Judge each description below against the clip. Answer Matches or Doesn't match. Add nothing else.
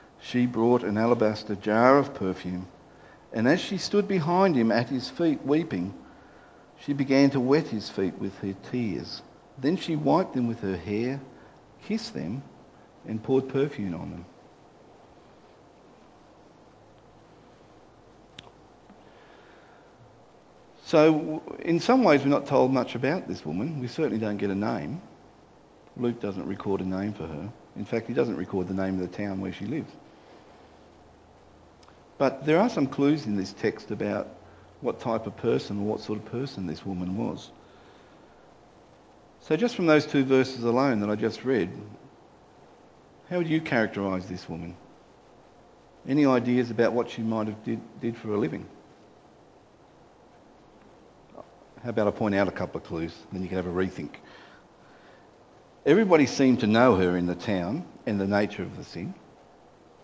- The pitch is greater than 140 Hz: Doesn't match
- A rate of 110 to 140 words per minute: Doesn't match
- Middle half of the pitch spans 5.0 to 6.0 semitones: Matches